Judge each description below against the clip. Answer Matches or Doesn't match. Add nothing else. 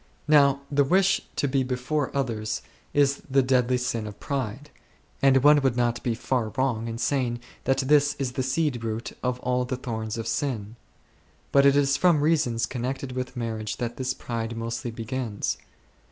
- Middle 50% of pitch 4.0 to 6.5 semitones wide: Doesn't match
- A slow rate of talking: Doesn't match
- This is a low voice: Matches